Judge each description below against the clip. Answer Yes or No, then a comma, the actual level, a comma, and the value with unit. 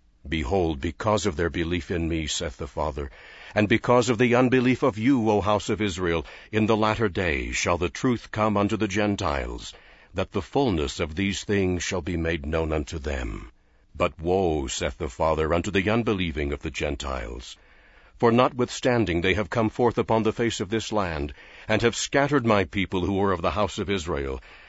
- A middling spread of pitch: Yes, average, 4.9 semitones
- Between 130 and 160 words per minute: No, average, 190 wpm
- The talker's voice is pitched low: Yes, low, 100 Hz